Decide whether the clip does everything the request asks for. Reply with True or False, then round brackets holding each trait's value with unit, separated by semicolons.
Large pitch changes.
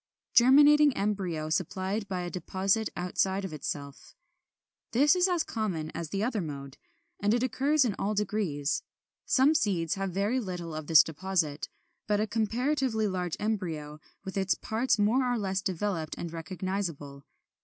False (5.0 semitones)